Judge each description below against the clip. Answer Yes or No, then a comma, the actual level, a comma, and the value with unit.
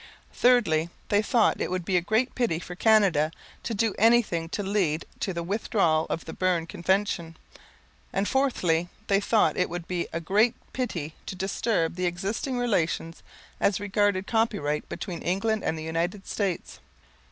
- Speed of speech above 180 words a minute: No, average, 165 wpm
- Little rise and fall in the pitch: No, average, 4.3 semitones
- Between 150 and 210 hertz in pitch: Yes, high, 190 Hz